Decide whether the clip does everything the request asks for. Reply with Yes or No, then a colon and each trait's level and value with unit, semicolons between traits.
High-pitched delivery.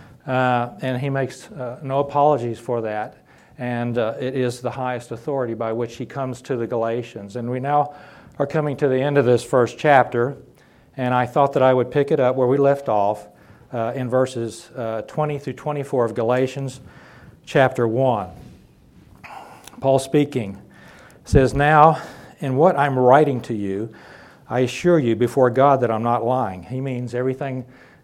No: low, 125 Hz